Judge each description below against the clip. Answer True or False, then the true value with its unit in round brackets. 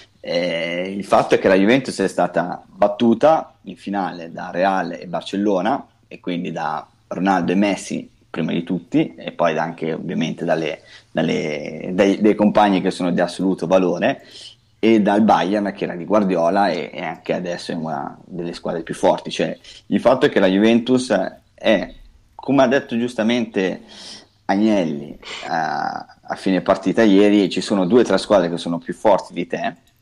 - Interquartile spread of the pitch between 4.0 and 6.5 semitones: False (3.3 semitones)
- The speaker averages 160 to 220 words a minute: True (165 wpm)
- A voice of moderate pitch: False (100 Hz)